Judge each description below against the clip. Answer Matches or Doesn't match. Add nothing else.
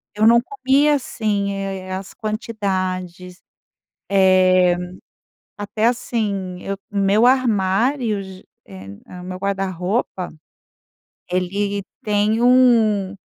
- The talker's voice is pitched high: Matches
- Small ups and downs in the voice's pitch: Doesn't match